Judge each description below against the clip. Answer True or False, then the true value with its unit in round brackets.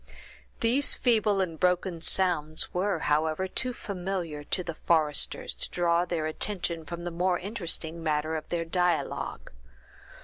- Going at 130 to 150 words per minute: True (140 wpm)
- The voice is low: False (175 Hz)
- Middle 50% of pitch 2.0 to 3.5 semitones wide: True (2.8 semitones)